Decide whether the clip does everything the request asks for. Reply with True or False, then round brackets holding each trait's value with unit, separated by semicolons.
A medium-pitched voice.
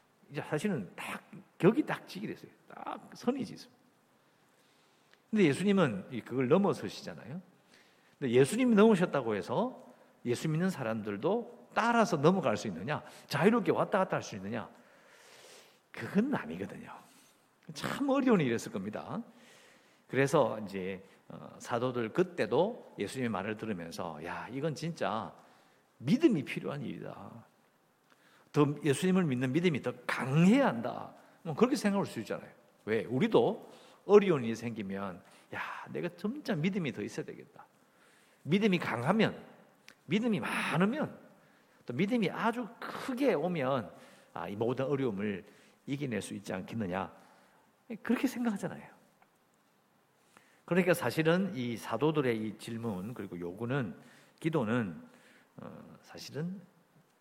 True (170 Hz)